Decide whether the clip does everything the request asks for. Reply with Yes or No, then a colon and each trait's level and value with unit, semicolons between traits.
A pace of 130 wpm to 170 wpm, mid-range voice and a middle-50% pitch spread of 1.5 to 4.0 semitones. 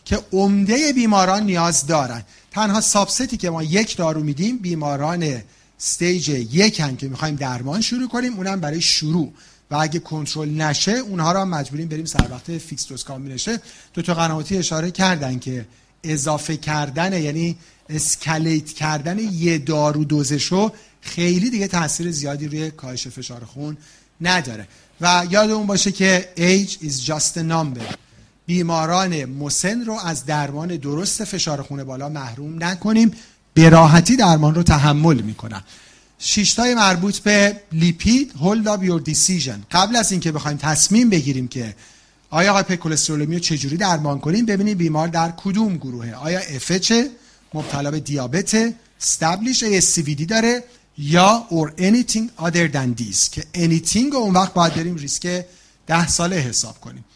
No: average, 145 wpm; medium, 165 Hz; average, 4.5 semitones